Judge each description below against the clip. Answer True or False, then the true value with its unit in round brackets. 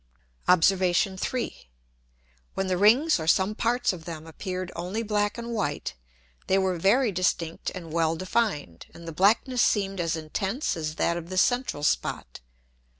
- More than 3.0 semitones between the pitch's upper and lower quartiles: True (4.1 semitones)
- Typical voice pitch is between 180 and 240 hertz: True (185 Hz)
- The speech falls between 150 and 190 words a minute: True (155 wpm)